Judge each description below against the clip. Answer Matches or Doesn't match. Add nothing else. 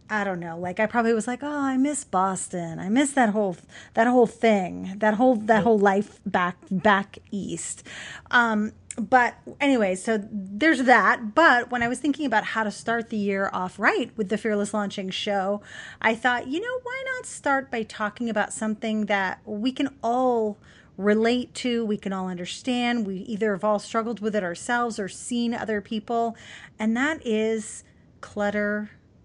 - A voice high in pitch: Matches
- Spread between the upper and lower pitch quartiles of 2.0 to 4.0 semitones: Matches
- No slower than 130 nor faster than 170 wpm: Doesn't match